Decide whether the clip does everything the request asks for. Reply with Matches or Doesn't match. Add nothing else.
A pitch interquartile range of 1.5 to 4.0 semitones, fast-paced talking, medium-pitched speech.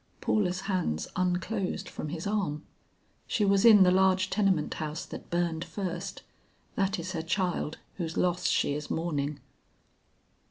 Doesn't match